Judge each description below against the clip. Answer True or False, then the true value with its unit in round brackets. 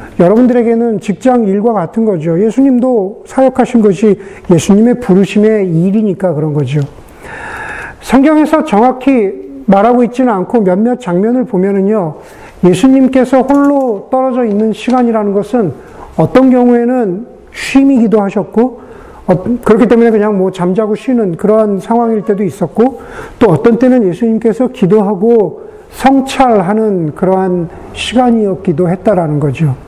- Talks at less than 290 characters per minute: False (310 characters per minute)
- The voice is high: True (220 Hz)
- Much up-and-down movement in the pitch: False (4.4 semitones)